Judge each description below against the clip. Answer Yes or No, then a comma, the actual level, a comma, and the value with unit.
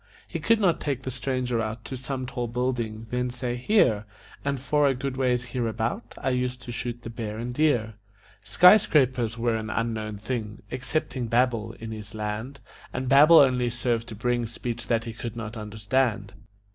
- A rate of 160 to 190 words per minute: Yes, average, 180 wpm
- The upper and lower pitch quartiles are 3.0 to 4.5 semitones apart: No, narrow, 2.5 semitones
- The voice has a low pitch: Yes, low, 120 Hz